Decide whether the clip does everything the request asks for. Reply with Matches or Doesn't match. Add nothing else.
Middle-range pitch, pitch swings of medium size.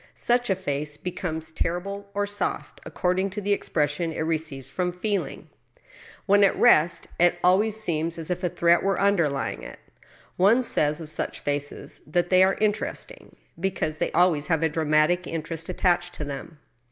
Matches